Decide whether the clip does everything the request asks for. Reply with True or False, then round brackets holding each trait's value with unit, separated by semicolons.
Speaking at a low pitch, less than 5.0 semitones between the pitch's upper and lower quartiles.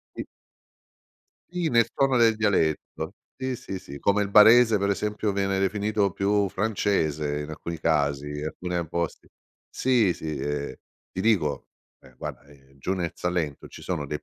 False (95 Hz; 5.8 semitones)